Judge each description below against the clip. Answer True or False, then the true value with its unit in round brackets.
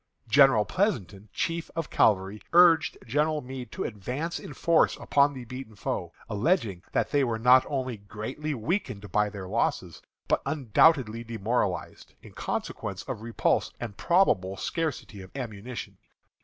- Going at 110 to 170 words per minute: True (140 wpm)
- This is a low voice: True (120 Hz)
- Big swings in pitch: True (6.1 semitones)